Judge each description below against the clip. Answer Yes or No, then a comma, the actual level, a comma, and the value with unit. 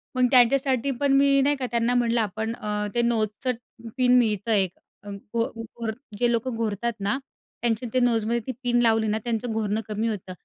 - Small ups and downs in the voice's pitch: Yes, narrow, 2.3 semitones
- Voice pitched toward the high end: Yes, high, 230 Hz